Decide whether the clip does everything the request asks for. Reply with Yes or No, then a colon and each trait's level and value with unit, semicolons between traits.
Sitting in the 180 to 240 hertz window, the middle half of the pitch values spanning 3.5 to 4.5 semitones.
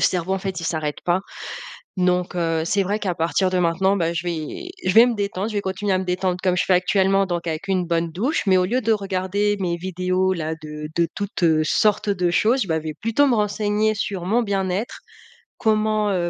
No: high, 190 Hz; average, 3.0 semitones